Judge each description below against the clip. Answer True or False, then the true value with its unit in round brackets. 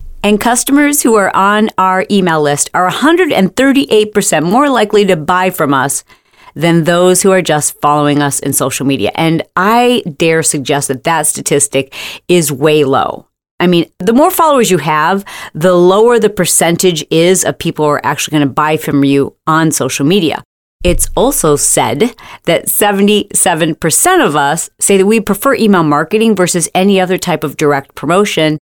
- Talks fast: False (170 wpm)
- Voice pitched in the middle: True (175 Hz)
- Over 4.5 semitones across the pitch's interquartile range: True (5.3 semitones)